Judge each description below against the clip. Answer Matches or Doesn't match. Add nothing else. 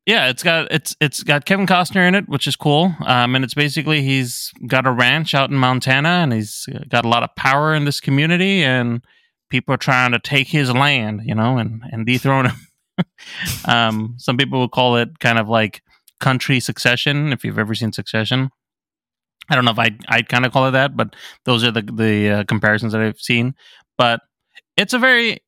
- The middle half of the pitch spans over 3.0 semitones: Matches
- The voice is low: Matches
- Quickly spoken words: Matches